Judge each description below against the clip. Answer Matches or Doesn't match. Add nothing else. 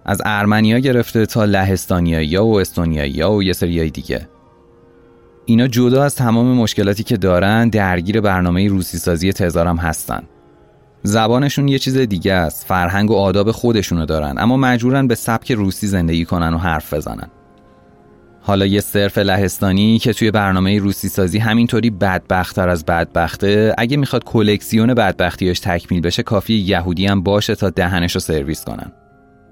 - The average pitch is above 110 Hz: Doesn't match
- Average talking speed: Matches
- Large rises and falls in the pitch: Doesn't match